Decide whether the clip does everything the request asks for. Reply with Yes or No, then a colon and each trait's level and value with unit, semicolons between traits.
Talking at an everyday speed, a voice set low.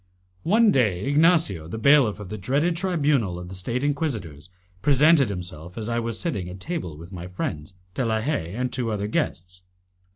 Yes: average, 185 wpm; low, 110 Hz